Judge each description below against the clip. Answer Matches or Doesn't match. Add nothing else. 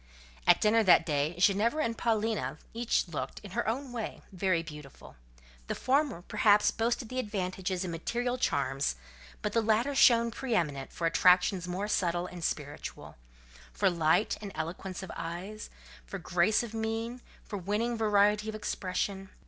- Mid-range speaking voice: Doesn't match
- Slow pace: Doesn't match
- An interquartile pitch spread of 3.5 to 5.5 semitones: Matches